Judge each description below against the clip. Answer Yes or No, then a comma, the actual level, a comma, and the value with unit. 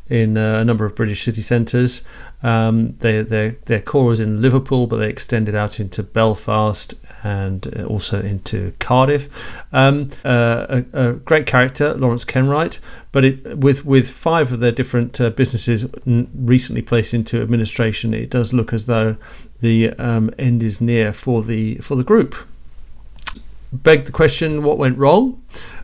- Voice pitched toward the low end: Yes, low, 120 Hz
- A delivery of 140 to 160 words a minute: Yes, average, 155 wpm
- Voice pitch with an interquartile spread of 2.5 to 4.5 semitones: Yes, average, 2.8 semitones